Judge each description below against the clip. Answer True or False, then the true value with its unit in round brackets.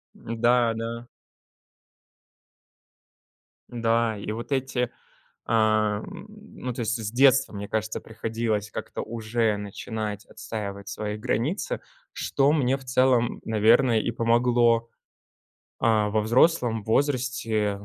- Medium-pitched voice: False (115 Hz)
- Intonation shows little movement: True (2.3 semitones)